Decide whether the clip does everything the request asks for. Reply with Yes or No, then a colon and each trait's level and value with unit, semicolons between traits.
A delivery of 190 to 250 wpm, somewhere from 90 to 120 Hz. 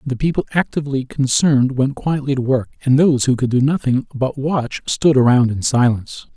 No: average, 200 wpm; low, 135 Hz